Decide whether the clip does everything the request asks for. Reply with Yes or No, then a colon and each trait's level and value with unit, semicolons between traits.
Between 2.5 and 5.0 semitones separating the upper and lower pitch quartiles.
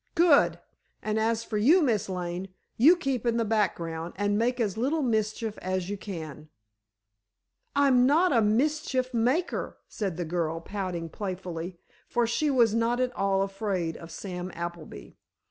No: wide, 5.5 semitones